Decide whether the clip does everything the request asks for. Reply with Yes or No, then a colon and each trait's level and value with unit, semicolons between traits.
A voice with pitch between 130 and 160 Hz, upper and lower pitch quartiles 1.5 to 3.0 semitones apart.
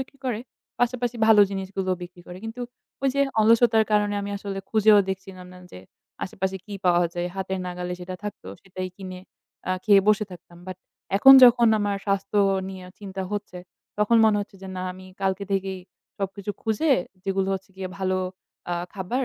No: high, 195 Hz; narrow, 2.4 semitones